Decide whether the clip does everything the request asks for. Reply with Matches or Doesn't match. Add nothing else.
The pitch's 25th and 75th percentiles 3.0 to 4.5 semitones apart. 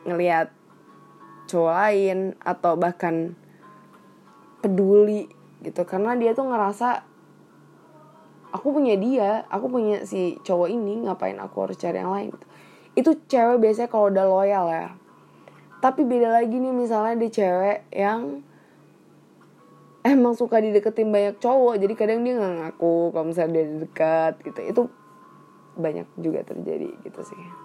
Doesn't match